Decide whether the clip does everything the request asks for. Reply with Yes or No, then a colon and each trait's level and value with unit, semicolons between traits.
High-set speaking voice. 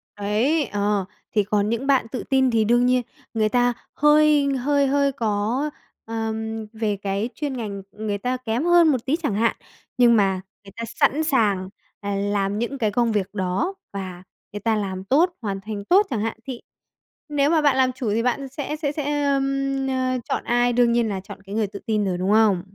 Yes: high, 230 Hz